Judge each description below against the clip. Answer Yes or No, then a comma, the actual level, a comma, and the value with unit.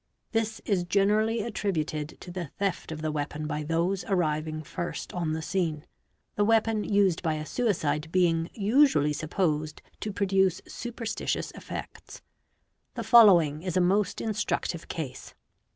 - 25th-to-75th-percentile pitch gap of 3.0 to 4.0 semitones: No, average, 4.9 semitones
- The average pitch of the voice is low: No, medium, 180 Hz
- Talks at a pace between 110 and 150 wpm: Yes, average, 140 wpm